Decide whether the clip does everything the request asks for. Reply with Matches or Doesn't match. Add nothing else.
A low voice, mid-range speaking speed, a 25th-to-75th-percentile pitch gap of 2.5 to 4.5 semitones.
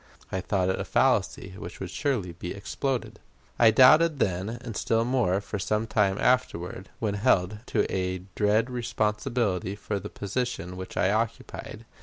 Matches